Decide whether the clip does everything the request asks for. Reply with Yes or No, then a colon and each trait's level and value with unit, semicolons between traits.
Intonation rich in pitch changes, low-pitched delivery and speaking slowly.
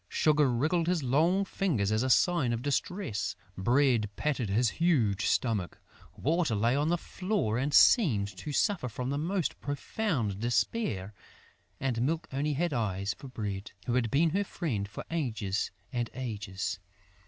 No: wide, 7.0 semitones; low, 130 Hz; average, 155 wpm